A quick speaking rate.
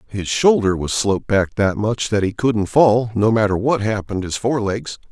Yes: fast, 210 wpm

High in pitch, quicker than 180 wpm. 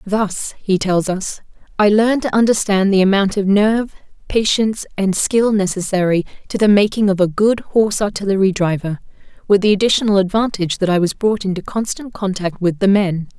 No: high, 200 Hz; average, 175 wpm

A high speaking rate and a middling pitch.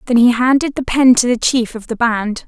No: fast, 265 wpm; high, 240 Hz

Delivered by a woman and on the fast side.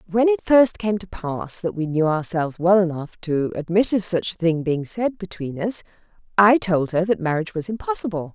Yes: female; fast, 210 wpm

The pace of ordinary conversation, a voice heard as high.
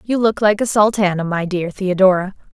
Yes: average, 190 wpm; high, 195 Hz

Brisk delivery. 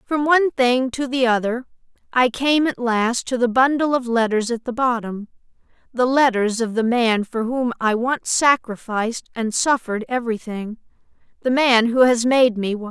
No: average, 180 wpm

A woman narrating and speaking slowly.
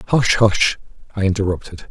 No: male; slow, 125 wpm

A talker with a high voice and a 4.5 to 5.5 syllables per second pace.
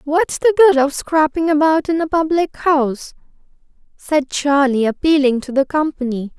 Yes: very high, 295 Hz; 4.6 syllables/s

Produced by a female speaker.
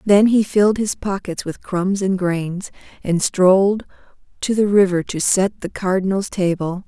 Yes: female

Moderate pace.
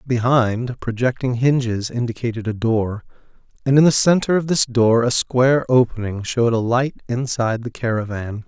Yes: average, 155 wpm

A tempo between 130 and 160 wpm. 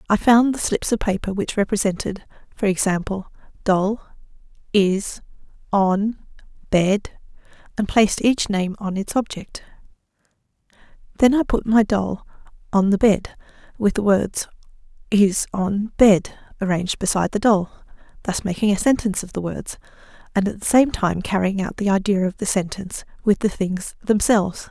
Yes: average, 150 wpm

